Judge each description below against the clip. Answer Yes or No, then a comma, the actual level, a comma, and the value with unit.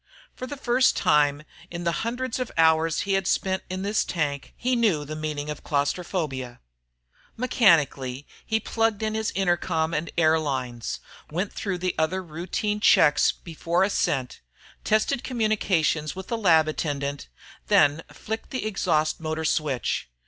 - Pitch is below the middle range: No, medium, 170 Hz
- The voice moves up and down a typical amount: No, wide, 5.7 semitones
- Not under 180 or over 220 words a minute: No, average, 145 wpm